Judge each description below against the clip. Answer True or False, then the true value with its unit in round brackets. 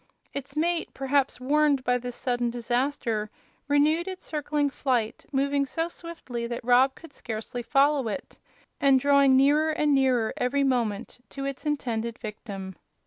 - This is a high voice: True (270 Hz)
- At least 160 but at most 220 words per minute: False (145 wpm)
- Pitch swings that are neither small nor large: True (3.1 semitones)